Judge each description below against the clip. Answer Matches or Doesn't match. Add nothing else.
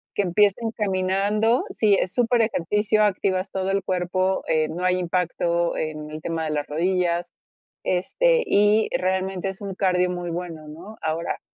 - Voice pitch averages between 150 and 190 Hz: Matches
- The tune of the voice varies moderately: Matches